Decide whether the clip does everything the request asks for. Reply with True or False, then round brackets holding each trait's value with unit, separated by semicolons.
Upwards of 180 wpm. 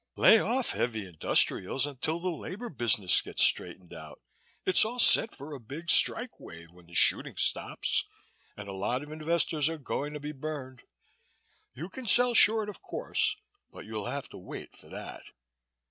False (175 wpm)